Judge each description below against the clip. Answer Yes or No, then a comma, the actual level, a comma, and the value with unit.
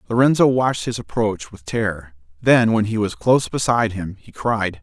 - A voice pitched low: Yes, low, 110 Hz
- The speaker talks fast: No, average, 185 wpm